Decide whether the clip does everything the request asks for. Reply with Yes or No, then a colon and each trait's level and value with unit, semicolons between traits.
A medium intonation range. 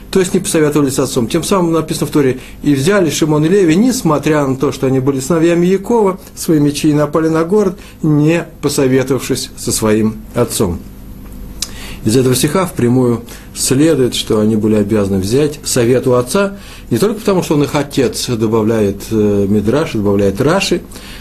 No: wide, 5.8 semitones